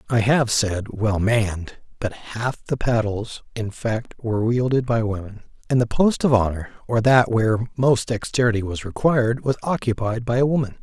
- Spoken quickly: No, average, 175 wpm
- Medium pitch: No, low, 115 Hz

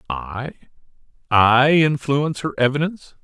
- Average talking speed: No, slow, 75 wpm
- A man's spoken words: Yes, male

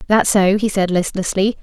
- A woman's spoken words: Yes, female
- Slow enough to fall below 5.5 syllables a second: Yes, 5.0 syllables/s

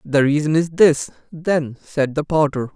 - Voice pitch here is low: No, medium, 150 Hz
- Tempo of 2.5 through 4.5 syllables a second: Yes, 4.3 syllables/s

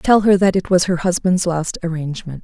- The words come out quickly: Yes, fast, 220 wpm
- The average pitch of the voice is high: No, medium, 175 Hz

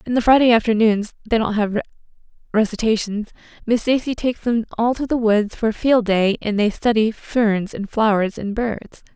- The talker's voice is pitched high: Yes, high, 220 Hz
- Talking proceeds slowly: No, average, 185 wpm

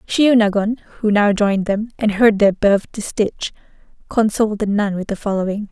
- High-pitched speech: Yes, high, 210 Hz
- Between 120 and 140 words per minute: No, average, 170 wpm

